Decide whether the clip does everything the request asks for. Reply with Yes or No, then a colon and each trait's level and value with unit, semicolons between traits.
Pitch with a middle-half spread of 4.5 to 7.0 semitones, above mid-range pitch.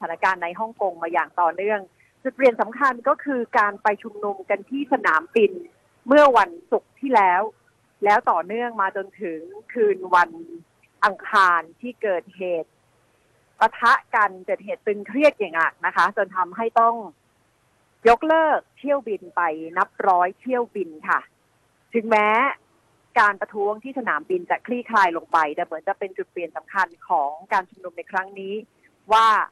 Yes: average, 5.3 semitones; high, 205 Hz